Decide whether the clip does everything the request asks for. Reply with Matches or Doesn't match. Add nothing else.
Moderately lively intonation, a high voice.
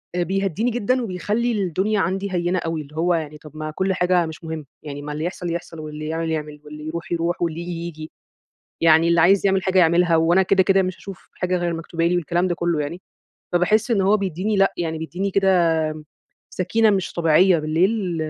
Doesn't match